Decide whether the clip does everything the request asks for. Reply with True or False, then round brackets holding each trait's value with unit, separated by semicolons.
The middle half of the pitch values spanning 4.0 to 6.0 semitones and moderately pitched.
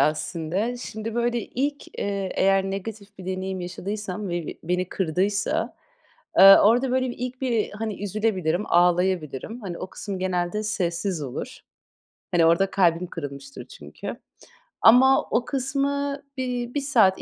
False (5.0 semitones; 200 Hz)